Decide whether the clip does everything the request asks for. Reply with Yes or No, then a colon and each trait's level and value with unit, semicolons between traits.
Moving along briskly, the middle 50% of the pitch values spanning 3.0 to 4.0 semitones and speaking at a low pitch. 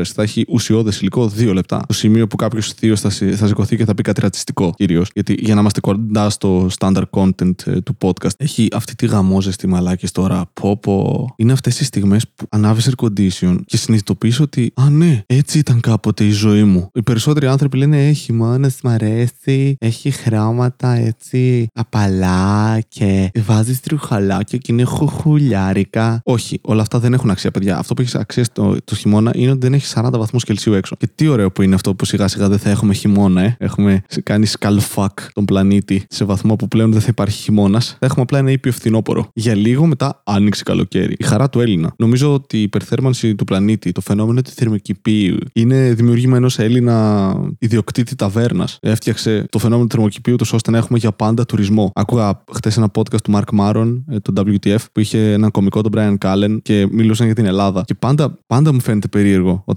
Yes: fast, 195 wpm; average, 3.3 semitones; low, 110 Hz